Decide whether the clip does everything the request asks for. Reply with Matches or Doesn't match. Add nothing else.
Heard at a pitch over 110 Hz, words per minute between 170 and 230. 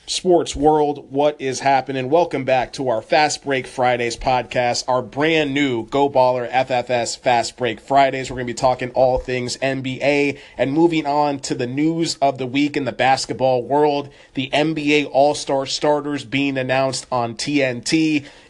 Doesn't match